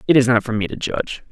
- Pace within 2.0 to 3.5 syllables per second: No, 7.3 syllables/s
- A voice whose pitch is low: Yes, low, 120 Hz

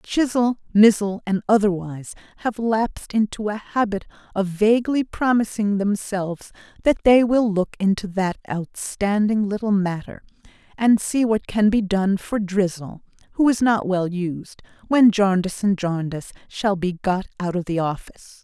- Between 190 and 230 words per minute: No, average, 145 wpm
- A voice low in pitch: No, high, 205 Hz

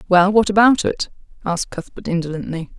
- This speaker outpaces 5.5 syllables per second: Yes, 5.9 syllables/s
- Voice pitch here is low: No, medium, 185 Hz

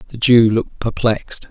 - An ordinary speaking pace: Yes, average, 160 wpm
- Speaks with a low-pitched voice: Yes, low, 115 Hz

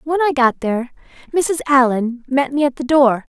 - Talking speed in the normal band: Yes, average, 195 wpm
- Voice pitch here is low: No, very high, 270 Hz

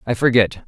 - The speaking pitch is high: No, low, 120 Hz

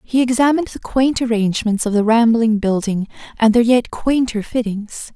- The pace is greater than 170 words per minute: No, average, 165 wpm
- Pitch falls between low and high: No, high, 230 Hz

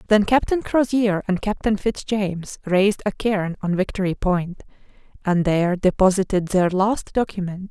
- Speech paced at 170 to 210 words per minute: No, average, 150 wpm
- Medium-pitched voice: No, high, 195 Hz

